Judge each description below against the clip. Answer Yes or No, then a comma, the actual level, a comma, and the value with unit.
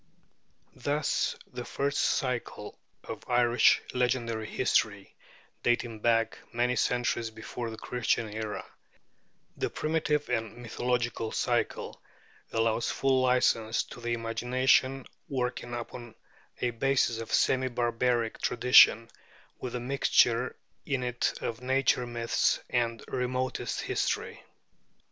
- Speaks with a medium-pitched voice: No, low, 120 Hz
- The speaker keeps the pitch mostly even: Yes, narrow, 1.7 semitones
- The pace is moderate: No, slow, 110 wpm